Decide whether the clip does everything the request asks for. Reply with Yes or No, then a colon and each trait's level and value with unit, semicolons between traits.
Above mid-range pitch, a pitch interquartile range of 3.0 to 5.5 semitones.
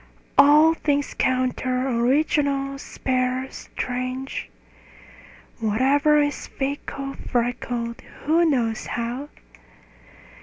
No: very high, 265 Hz; narrow, 2.4 semitones